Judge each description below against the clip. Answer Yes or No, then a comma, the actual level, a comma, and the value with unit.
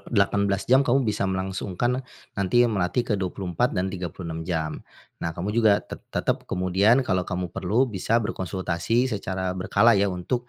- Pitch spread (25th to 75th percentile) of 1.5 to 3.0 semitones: Yes, narrow, 2.4 semitones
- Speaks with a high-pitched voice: No, very low, 95 Hz